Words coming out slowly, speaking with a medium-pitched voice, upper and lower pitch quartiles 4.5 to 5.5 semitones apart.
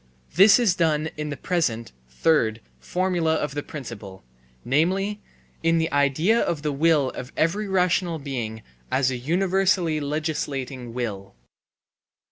Yes: slow, 130 wpm; medium, 155 Hz; average, 5.1 semitones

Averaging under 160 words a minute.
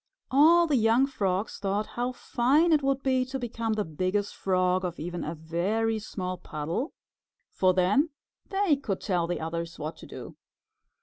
No: average, 170 wpm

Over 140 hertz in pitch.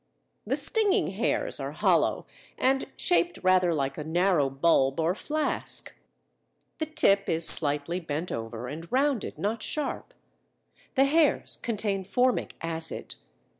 Yes: medium, 185 Hz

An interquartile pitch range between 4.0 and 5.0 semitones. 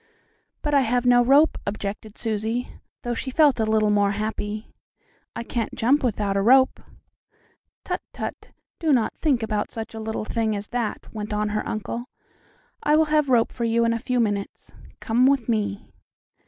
No: average, 2.9 semitones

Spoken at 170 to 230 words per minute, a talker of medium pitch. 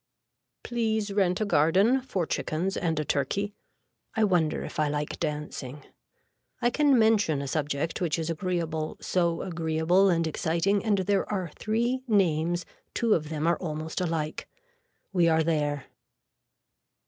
No: average, 145 wpm; medium, 170 Hz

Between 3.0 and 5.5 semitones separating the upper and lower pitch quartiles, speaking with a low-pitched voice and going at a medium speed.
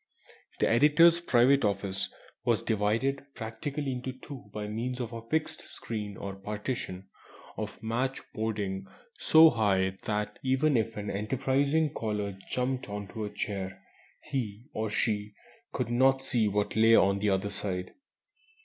Yes: average, 4.3 semitones; low, 110 Hz; average, 145 wpm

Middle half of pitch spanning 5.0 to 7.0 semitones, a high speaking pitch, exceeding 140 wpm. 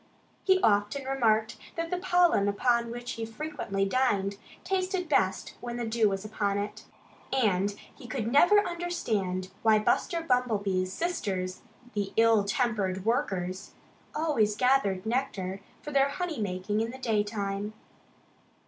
No: average, 5.3 semitones; high, 225 Hz; slow, 135 wpm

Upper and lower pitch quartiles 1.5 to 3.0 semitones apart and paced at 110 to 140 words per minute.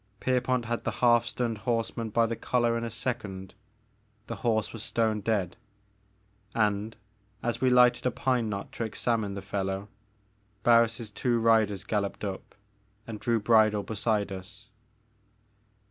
No: narrow, 2.4 semitones; average, 150 wpm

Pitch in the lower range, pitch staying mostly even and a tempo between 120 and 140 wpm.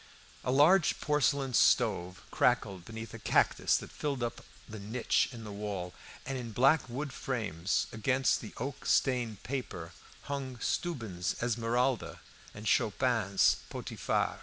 No: low, 120 Hz; average, 4.1 semitones; slow, 135 wpm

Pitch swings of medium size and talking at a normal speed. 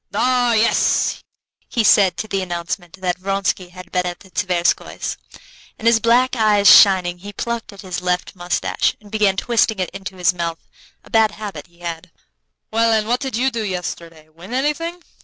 Yes: average, 4.0 semitones; average, 180 wpm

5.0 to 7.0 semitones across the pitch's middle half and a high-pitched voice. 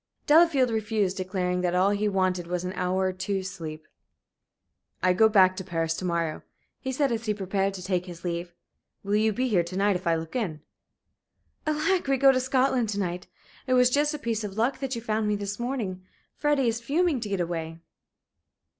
Yes: wide, 5.4 semitones; high, 200 Hz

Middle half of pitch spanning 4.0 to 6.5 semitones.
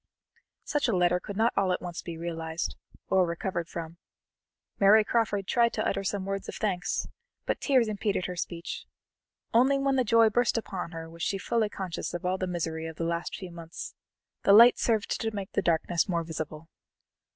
Yes: average, 4.4 semitones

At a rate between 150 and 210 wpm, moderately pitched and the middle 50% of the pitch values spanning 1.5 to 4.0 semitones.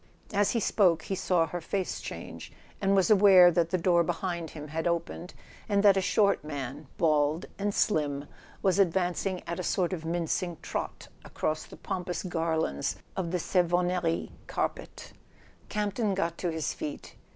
Yes: average, 170 wpm; medium, 175 Hz; average, 2.9 semitones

